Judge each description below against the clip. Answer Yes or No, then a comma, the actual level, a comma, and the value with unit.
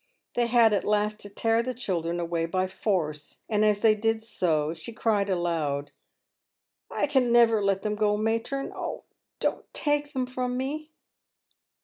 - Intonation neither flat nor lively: Yes, average, 4.3 semitones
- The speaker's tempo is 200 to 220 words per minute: No, average, 165 wpm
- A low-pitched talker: No, high, 215 Hz